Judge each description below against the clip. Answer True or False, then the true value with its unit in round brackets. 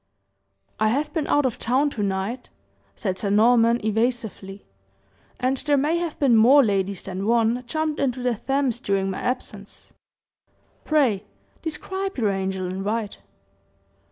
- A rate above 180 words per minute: False (145 wpm)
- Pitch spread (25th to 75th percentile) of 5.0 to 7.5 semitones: True (5.3 semitones)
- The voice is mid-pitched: False (235 Hz)